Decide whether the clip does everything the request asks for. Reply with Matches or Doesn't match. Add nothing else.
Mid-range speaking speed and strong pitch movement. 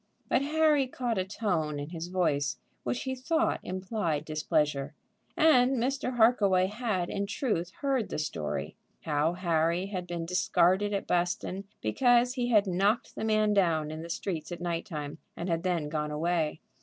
Matches